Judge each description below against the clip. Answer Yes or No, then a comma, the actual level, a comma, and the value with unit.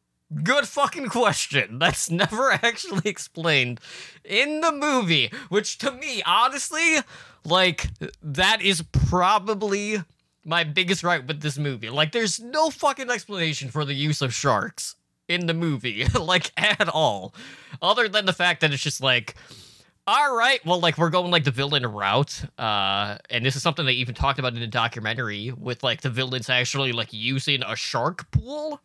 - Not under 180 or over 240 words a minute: No, average, 165 wpm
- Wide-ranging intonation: Yes, wide, 8.0 semitones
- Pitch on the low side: No, medium, 160 Hz